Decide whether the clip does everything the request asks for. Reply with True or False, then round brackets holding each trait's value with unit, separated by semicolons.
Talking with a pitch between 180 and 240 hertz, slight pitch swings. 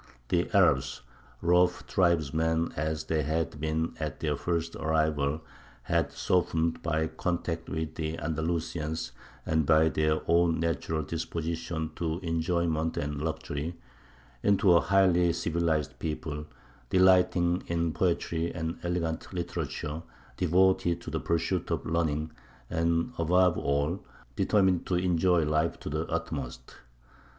False (80 Hz; 1.8 semitones)